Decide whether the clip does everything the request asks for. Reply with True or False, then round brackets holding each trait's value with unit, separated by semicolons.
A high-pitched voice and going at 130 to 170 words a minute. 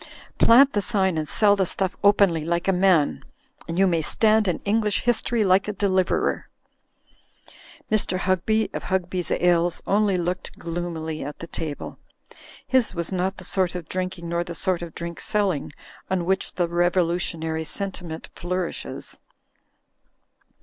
False (180 Hz; 150 wpm)